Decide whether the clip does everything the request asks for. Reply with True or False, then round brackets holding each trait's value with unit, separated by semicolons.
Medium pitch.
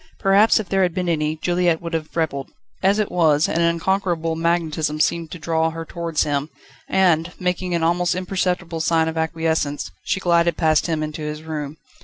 True (165 Hz)